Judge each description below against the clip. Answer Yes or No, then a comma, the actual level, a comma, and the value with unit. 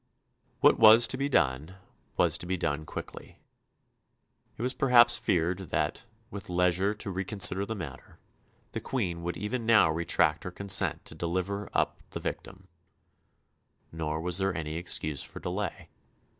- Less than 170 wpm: Yes, average, 150 wpm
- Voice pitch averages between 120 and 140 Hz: No, very low, 95 Hz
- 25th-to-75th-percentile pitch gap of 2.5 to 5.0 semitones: Yes, average, 3.6 semitones